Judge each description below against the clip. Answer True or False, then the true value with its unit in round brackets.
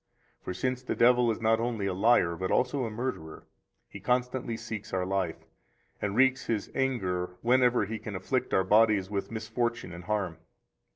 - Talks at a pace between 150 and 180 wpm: True (175 wpm)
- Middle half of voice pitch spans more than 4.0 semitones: True (4.4 semitones)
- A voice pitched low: True (110 Hz)